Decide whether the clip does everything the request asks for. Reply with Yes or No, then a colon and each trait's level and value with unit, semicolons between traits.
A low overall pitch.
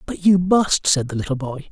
No: medium, 160 Hz